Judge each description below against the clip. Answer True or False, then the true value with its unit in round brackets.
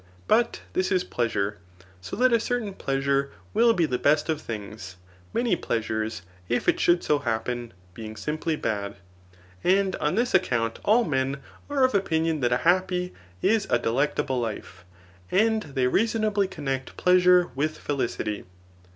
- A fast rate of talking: False (150 wpm)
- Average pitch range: False (7.9 semitones)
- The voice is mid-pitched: True (150 Hz)